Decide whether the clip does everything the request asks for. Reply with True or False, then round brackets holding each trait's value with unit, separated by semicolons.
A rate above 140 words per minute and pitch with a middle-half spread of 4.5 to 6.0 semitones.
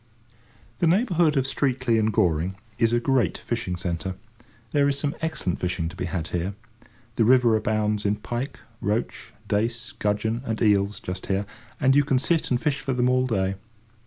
True (180 wpm; 5.3 semitones)